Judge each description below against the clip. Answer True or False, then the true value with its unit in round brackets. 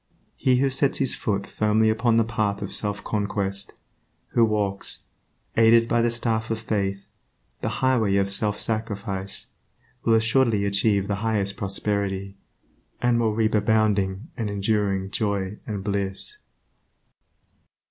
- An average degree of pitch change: False (2.3 semitones)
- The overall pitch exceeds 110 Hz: False (105 Hz)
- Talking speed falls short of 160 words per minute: True (135 wpm)